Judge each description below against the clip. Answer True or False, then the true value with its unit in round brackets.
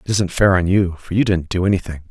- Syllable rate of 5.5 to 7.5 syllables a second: True (6.3 syllables/s)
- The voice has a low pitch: True (90 Hz)